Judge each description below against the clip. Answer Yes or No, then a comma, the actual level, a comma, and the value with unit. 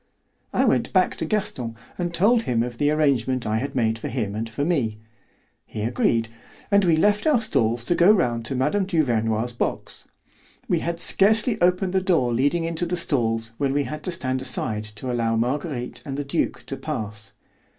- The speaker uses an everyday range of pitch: No, wide, 7.0 semitones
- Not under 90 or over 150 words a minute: No, average, 190 wpm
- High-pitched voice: No, low, 135 Hz